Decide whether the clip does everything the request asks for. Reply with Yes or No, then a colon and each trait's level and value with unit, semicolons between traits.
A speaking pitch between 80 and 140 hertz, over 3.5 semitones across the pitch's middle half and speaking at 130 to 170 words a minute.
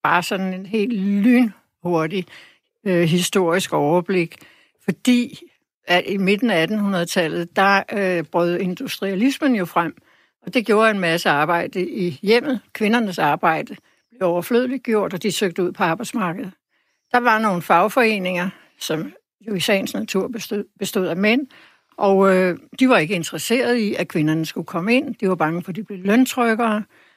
No: high, 195 Hz; average, 4.5 semitones; average, 160 wpm